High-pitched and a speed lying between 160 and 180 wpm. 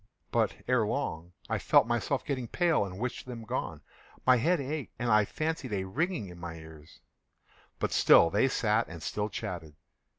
No: low, 115 Hz; average, 175 wpm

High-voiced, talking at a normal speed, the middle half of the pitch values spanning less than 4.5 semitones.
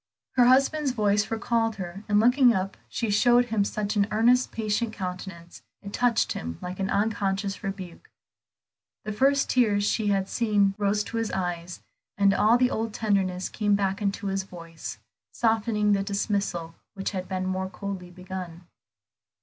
Yes: high, 205 Hz; average, 160 wpm; average, 2.9 semitones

